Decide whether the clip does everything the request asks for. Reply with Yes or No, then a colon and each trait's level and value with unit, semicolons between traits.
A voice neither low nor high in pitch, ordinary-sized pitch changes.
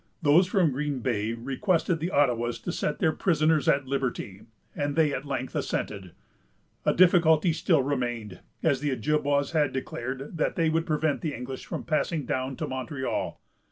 Yes: medium, 145 Hz; average, 3.6 semitones